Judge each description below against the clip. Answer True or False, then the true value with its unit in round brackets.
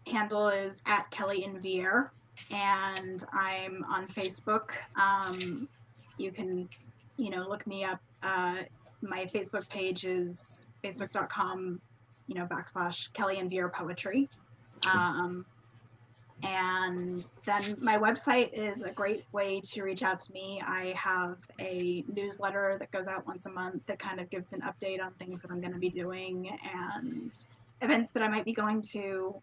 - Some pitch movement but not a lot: False (1.9 semitones)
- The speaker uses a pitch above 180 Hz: True (190 Hz)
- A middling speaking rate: True (155 wpm)